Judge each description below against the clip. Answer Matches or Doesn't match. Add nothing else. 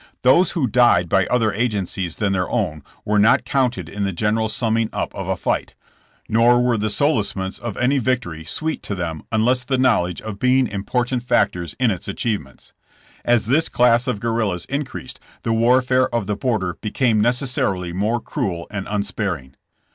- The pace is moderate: Matches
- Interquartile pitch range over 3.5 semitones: Matches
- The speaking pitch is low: Matches